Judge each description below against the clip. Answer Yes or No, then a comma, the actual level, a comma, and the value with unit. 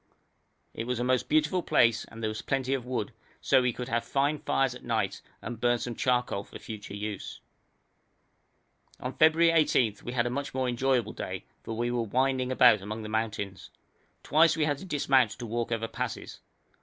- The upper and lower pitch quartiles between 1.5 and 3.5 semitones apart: Yes, average, 3.0 semitones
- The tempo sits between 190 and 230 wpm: Yes, average, 195 wpm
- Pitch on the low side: Yes, low, 125 Hz